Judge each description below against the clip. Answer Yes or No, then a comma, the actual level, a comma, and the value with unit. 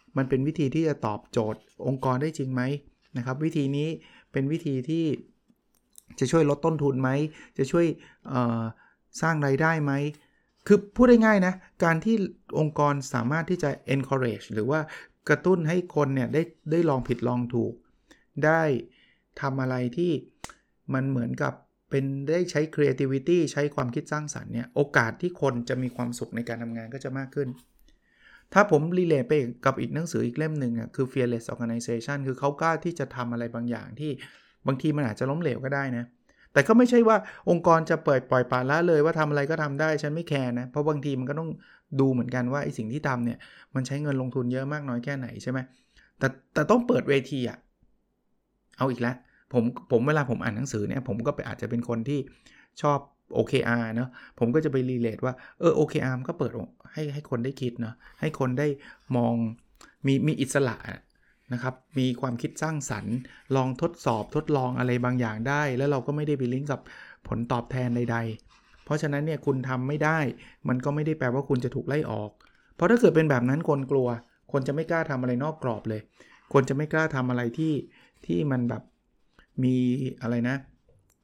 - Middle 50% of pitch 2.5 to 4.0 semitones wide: Yes, average, 3.5 semitones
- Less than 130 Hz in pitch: No, low, 135 Hz